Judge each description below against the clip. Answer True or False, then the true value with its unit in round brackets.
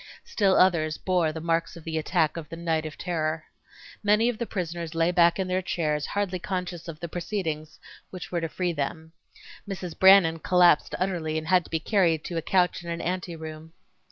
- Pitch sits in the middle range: True (170 Hz)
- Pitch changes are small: True (2.3 semitones)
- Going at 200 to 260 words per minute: True (205 wpm)